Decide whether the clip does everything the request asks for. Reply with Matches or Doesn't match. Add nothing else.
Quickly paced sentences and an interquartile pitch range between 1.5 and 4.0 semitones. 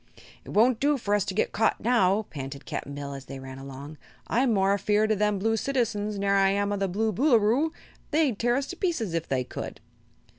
Doesn't match